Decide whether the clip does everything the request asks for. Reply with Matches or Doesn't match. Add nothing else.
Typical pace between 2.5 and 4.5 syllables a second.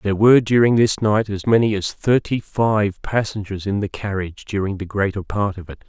Doesn't match